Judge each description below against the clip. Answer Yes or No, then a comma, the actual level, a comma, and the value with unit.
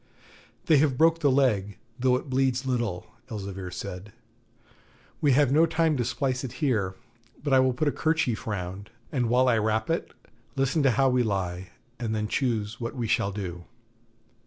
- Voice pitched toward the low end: Yes, low, 125 Hz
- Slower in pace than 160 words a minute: No, average, 180 wpm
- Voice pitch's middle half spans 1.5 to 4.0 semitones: No, average, 4.7 semitones